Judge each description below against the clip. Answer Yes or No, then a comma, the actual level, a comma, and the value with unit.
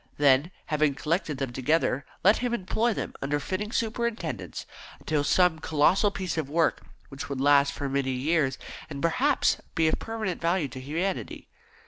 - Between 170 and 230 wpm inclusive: No, average, 160 wpm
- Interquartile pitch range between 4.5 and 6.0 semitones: Yes, average, 5.2 semitones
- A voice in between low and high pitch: Yes, medium, 160 Hz